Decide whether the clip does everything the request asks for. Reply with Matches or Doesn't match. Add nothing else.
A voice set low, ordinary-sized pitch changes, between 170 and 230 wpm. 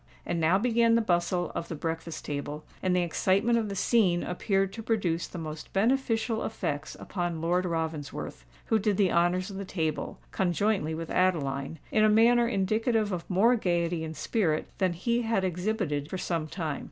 Doesn't match